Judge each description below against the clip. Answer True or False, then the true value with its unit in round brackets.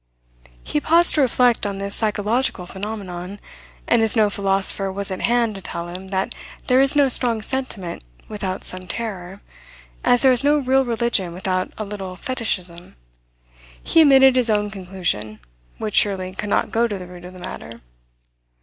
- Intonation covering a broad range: False (4.6 semitones)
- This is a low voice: False (205 Hz)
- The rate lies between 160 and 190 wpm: True (170 wpm)